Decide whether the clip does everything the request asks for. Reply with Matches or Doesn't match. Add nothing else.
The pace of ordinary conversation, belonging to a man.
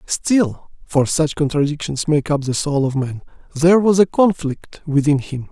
Matches